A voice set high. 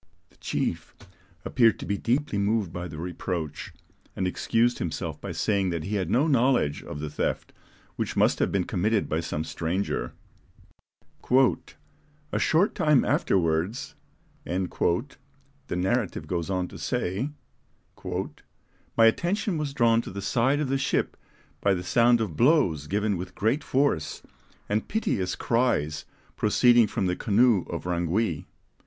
No: low, 100 Hz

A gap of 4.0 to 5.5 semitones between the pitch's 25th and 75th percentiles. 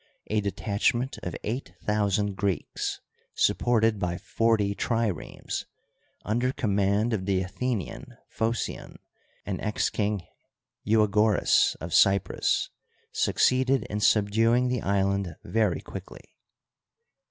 No: narrow, 2.4 semitones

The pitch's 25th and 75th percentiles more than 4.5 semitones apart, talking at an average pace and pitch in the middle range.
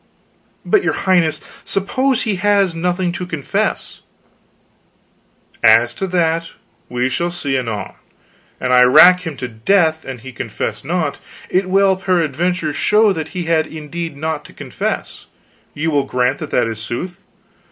Yes: wide, 5.4 semitones; average, 150 wpm; medium, 165 Hz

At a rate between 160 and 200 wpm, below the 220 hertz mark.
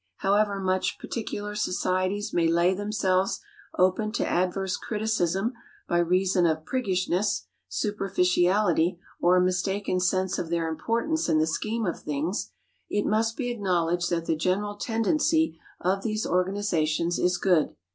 No: slow, 135 wpm; medium, 185 Hz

